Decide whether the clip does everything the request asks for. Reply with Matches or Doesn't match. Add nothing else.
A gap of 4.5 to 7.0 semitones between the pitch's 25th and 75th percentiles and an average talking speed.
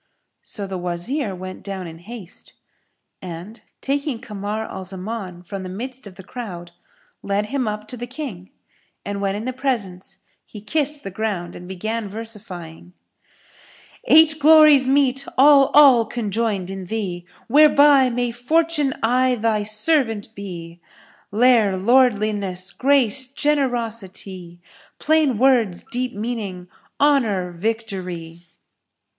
Doesn't match